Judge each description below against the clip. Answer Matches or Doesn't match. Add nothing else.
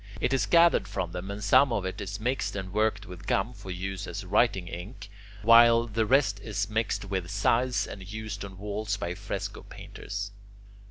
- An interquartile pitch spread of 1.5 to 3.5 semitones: Matches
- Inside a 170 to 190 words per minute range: Matches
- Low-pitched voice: Matches